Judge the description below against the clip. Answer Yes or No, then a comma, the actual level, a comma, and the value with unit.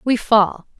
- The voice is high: Yes, high, 220 Hz